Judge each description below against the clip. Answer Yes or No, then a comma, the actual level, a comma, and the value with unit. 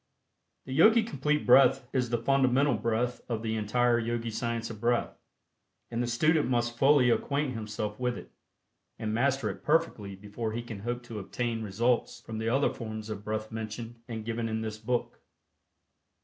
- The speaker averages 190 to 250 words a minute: No, average, 175 wpm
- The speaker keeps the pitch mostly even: Yes, narrow, 2.2 semitones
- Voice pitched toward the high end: No, low, 120 Hz